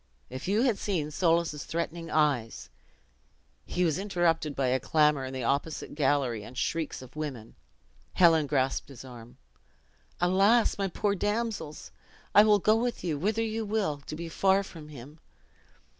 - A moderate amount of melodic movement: No, wide, 6.0 semitones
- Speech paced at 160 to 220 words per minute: Yes, average, 165 wpm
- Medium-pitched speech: Yes, medium, 160 Hz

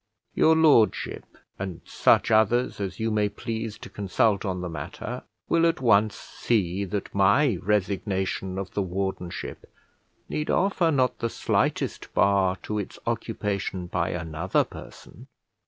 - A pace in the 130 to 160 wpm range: Yes, average, 140 wpm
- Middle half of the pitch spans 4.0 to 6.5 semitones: No, average, 3.4 semitones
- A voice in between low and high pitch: No, low, 100 Hz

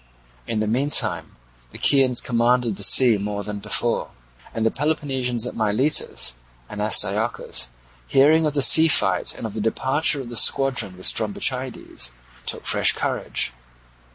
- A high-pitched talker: No, low, 120 Hz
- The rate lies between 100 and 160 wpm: Yes, average, 150 wpm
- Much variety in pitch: No, average, 4.2 semitones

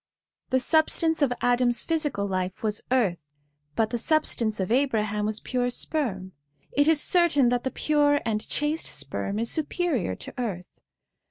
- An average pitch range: No, wide, 5.9 semitones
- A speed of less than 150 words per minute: No, average, 155 wpm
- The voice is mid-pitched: No, high, 245 Hz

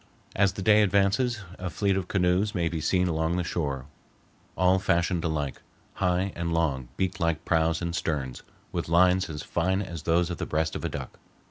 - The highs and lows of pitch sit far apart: No, narrow, 2.6 semitones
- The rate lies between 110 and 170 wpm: No, average, 195 wpm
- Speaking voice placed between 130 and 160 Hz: No, very low, 85 Hz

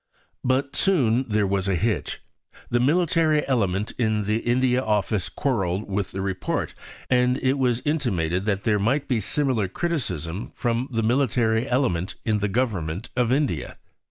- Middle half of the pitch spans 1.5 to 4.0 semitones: No, average, 4.7 semitones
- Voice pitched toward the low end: Yes, low, 115 Hz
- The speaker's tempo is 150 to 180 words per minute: Yes, average, 155 wpm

